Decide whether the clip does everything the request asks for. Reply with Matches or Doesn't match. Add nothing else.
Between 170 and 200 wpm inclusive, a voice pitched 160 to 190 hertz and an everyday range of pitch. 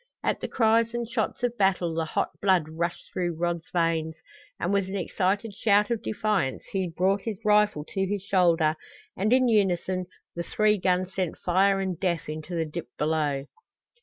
Matches